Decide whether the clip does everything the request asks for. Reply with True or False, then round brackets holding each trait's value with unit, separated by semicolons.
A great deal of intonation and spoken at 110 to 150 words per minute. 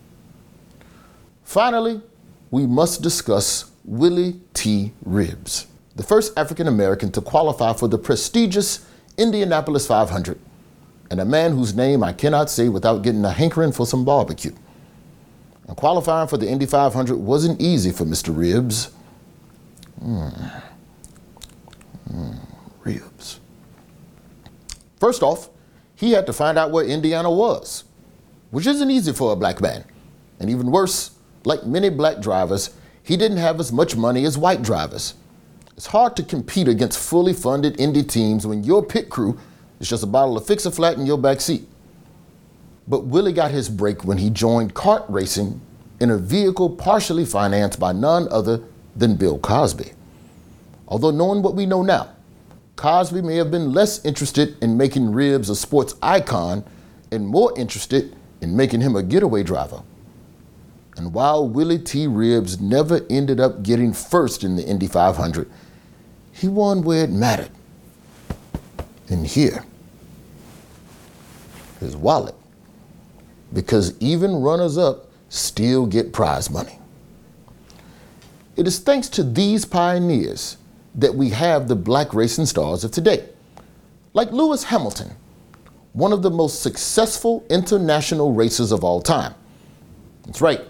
True (7.4 semitones; 140 wpm)